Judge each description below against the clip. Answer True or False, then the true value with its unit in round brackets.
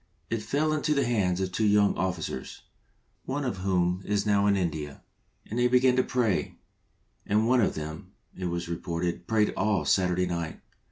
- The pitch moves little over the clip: False (4.6 semitones)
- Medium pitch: False (100 Hz)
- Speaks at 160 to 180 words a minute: True (175 wpm)